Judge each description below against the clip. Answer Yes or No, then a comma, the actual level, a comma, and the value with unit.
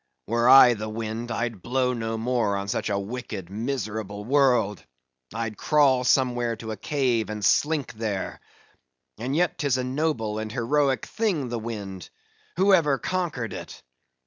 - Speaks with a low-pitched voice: Yes, low, 120 Hz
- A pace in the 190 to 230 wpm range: No, average, 155 wpm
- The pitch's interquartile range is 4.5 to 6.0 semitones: No, average, 3.7 semitones